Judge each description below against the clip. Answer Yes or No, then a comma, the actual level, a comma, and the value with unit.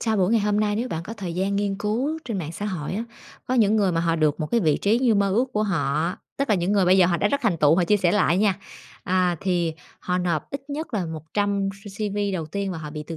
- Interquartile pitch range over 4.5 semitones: No, average, 3.5 semitones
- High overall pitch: Yes, high, 195 Hz